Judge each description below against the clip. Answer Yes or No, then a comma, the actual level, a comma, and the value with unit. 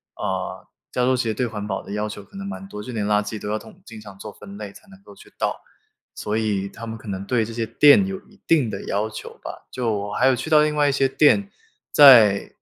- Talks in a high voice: No, low, 110 Hz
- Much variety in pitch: No, average, 4.8 semitones